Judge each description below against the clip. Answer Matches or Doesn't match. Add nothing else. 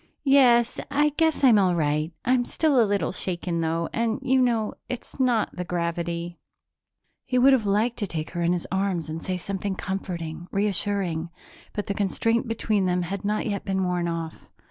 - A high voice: Matches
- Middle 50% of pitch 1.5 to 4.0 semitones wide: Doesn't match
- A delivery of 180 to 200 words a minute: Matches